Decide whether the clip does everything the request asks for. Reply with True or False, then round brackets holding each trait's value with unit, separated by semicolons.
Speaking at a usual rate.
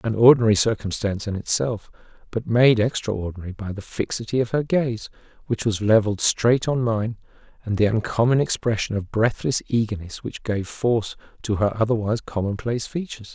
True (155 wpm)